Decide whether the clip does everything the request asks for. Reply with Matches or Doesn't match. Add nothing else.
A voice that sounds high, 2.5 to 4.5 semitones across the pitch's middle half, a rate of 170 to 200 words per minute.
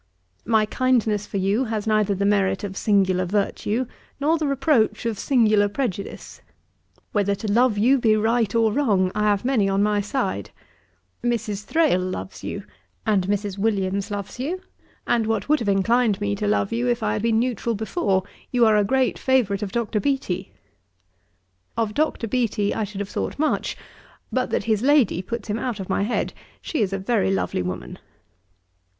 Matches